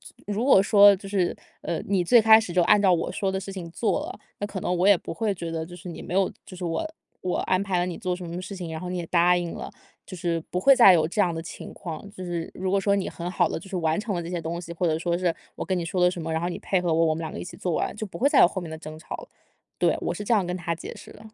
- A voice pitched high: No, medium, 180 Hz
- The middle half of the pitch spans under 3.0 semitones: Yes, narrow, 2.6 semitones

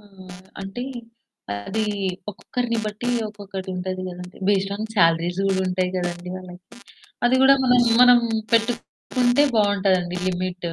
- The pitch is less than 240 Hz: Yes, high, 190 Hz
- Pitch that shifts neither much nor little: Yes, average, 3.7 semitones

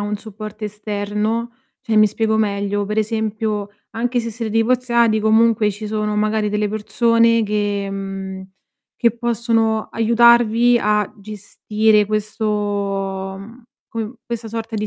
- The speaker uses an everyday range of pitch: No, narrow, 1.6 semitones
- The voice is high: Yes, high, 215 Hz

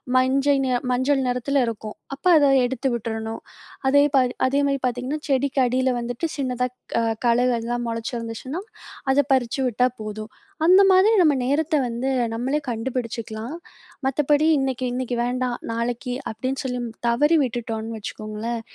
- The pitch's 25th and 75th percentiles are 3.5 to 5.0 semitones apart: No, average, 2.7 semitones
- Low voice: No, very high, 250 Hz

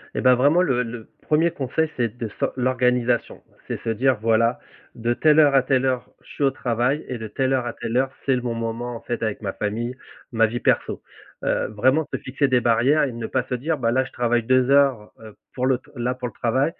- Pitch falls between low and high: No, low, 125 Hz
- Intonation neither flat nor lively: No, narrow, 2.3 semitones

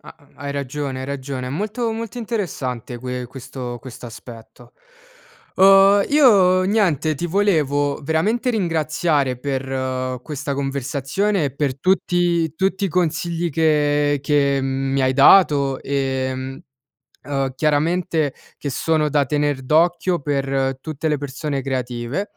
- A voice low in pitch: No, medium, 145 Hz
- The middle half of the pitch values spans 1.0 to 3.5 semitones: No, average, 4.5 semitones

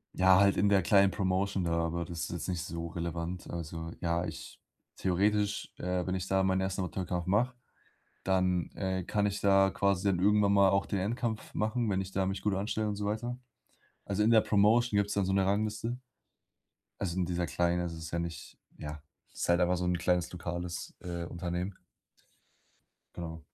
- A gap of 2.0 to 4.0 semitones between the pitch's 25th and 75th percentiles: Yes, narrow, 2.6 semitones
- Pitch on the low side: Yes, very low, 95 Hz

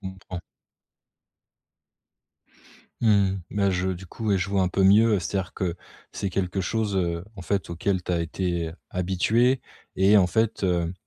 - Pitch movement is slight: Yes, narrow, 2.0 semitones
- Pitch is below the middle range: Yes, very low, 95 Hz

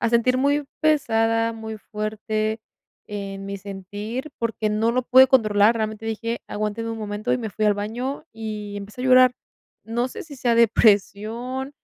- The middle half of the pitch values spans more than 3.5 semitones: No, average, 2.7 semitones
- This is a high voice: Yes, high, 225 Hz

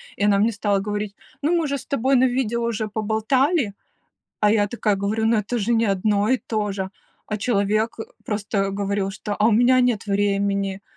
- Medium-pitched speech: No, high, 210 Hz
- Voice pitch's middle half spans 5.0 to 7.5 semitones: No, average, 2.7 semitones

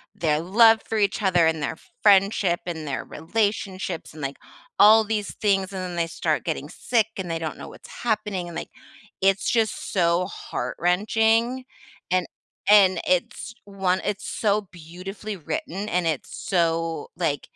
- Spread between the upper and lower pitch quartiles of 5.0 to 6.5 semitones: No, average, 3.7 semitones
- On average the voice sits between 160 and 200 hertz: Yes, medium, 185 Hz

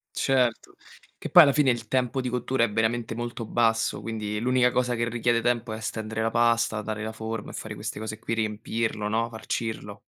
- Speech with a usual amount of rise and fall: No, narrow, 1.4 semitones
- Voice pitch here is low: Yes, low, 115 Hz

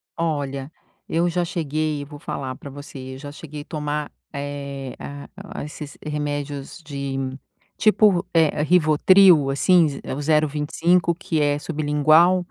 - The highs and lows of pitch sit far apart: No, narrow, 2.5 semitones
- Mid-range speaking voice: Yes, medium, 150 Hz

